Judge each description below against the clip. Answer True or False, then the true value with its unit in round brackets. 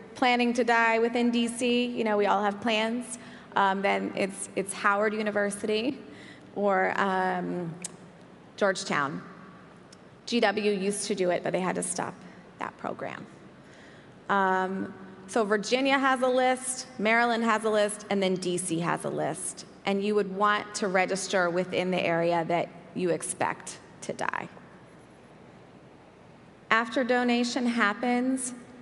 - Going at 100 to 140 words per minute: True (135 wpm)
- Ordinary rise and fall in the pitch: True (3.9 semitones)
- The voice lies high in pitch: True (210 Hz)